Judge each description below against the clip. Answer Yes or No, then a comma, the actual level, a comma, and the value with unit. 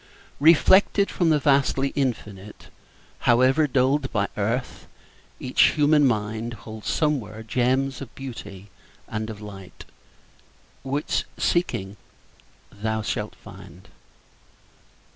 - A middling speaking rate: No, slow, 100 wpm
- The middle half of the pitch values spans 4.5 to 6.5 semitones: Yes, average, 4.8 semitones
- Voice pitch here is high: No, low, 125 Hz